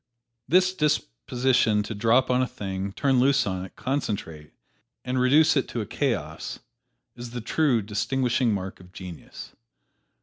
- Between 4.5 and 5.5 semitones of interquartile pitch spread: Yes, average, 5.0 semitones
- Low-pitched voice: Yes, low, 120 Hz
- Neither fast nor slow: Yes, average, 145 wpm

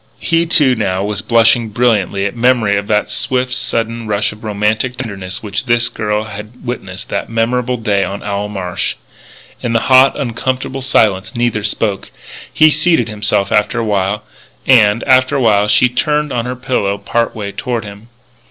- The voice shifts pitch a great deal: No, average, 3.4 semitones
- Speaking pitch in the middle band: No, low, 115 Hz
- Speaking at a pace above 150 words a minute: Yes, average, 170 wpm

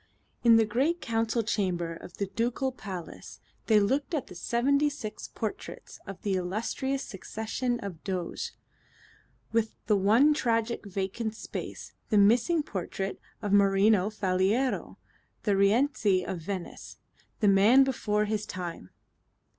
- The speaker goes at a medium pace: No, slow, 130 wpm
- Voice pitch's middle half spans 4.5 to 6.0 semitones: No, average, 3.6 semitones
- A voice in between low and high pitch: No, high, 215 Hz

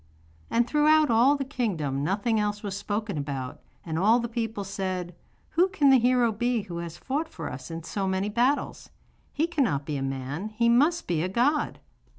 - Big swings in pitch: Yes, wide, 6.4 semitones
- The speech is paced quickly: No, average, 190 wpm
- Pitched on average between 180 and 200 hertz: No, high, 215 Hz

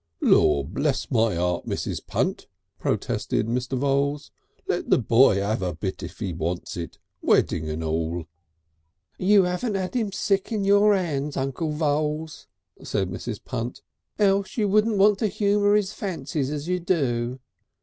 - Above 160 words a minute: No, average, 155 wpm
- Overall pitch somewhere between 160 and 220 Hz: No, medium, 140 Hz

